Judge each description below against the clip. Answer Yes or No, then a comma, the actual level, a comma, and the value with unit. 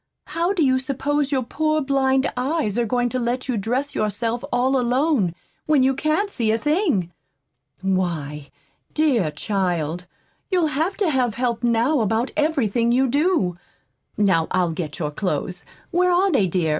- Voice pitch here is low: No, high, 245 Hz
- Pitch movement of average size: No, wide, 7.0 semitones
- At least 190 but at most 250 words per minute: No, average, 160 wpm